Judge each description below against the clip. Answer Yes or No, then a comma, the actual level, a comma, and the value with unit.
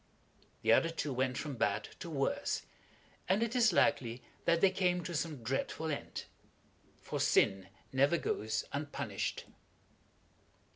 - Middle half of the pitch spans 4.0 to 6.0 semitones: Yes, average, 5.1 semitones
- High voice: No, medium, 145 Hz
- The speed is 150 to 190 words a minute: No, slow, 135 wpm